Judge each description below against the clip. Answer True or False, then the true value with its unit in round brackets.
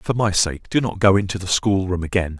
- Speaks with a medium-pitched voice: False (95 Hz)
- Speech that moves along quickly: True (250 wpm)